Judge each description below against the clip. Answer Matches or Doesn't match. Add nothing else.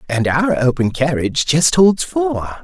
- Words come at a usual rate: Matches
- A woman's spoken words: Doesn't match